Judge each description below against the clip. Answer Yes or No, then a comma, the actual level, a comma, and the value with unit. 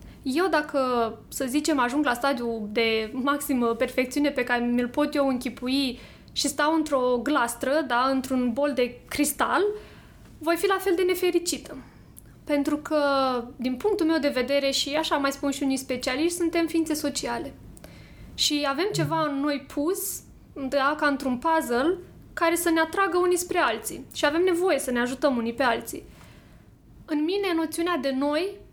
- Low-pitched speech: No, very high, 290 Hz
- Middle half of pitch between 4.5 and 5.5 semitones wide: No, average, 3.9 semitones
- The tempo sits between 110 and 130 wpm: No, average, 165 wpm